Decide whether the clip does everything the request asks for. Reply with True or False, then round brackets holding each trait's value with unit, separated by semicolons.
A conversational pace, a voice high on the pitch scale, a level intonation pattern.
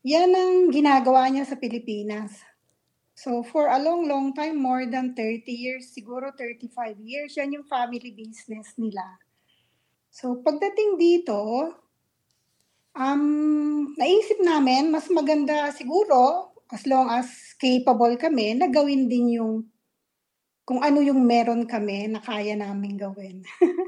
False (130 wpm; 255 Hz; 4.2 semitones)